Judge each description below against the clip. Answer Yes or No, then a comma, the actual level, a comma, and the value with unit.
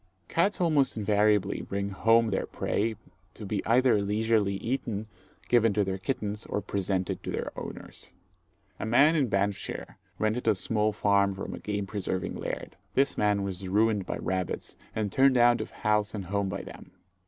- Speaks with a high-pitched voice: No, low, 105 Hz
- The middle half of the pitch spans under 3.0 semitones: Yes, narrow, 2.4 semitones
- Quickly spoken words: No, average, 170 wpm